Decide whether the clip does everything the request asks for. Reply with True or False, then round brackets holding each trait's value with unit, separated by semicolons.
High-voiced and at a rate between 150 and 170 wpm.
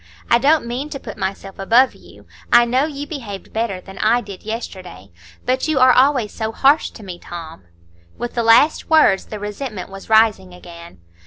False (225 Hz; 185 wpm)